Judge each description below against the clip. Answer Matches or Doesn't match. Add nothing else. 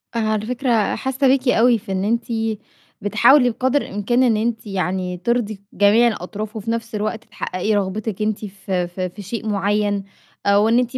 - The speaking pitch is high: Matches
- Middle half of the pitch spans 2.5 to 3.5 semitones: Matches